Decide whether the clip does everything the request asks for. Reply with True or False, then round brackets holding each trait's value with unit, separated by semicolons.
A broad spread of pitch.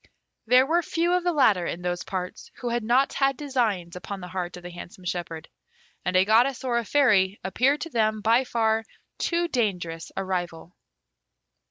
True (6.4 semitones)